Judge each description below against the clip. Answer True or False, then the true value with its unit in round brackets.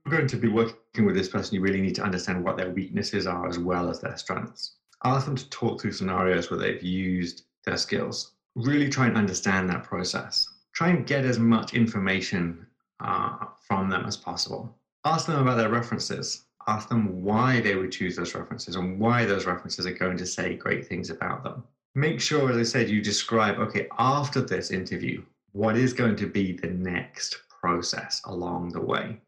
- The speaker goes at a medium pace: True (195 wpm)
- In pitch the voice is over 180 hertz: False (105 Hz)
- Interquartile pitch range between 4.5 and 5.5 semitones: True (5.1 semitones)